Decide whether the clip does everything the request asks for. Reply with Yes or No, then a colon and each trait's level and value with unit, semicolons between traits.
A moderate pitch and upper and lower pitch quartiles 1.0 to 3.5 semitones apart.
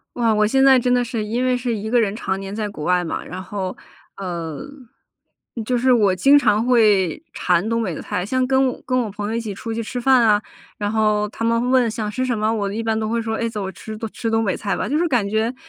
No: high, 220 Hz; average, 3.0 semitones